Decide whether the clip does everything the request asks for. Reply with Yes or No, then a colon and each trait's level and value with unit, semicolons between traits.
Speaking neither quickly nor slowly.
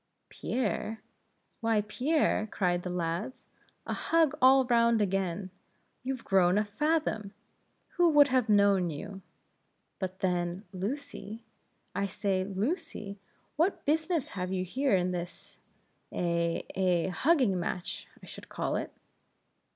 No: slow, 125 wpm